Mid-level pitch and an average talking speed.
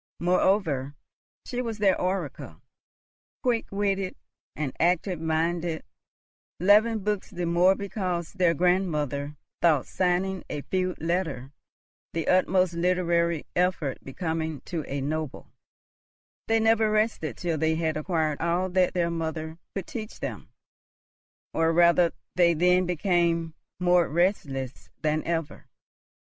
No: medium, 175 Hz; slow, 120 wpm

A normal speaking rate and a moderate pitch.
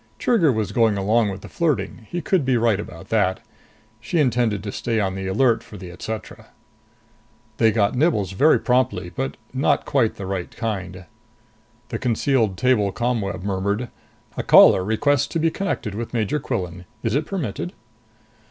No: average, 165 wpm; low, 110 Hz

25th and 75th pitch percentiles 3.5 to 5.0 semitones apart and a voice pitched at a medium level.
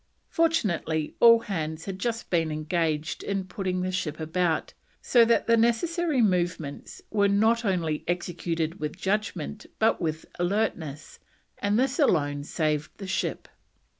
No: wide, 5.6 semitones; medium, 180 Hz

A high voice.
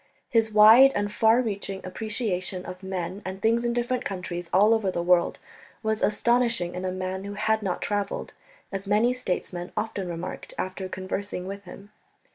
Yes: high, 200 Hz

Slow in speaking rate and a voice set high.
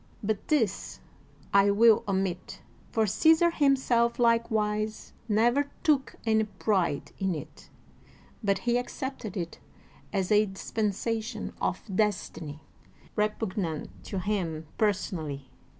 Yes: slow, 110 wpm; high, 210 Hz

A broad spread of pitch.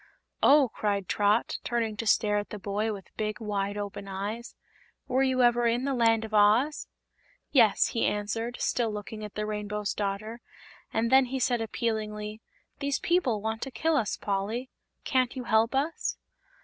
No: average, 2.7 semitones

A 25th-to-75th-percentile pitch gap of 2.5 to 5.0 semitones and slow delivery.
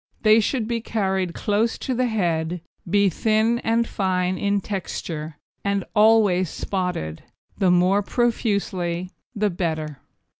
Yes: average, 3.6 semitones; slow, 125 wpm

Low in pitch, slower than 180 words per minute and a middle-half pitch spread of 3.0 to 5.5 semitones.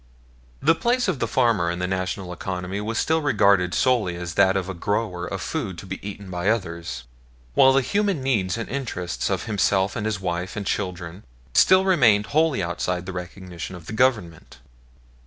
No: very low, 95 Hz; average, 185 wpm; average, 4.8 semitones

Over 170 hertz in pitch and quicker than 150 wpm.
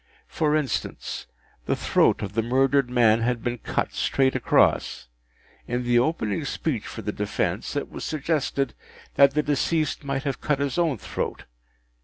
No: low, 135 Hz; average, 160 wpm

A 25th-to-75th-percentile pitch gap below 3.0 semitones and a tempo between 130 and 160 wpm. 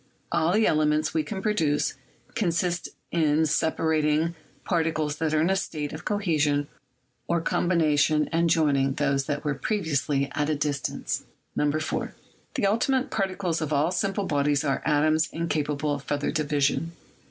Yes: narrow, 2.4 semitones; average, 145 wpm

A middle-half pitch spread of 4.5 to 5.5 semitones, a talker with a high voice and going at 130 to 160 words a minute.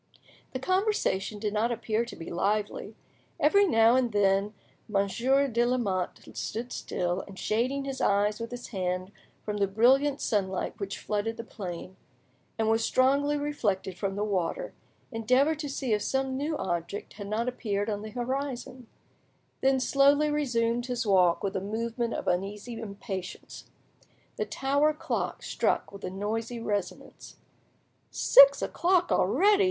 Yes: average, 4.9 semitones; high, 225 Hz; average, 150 wpm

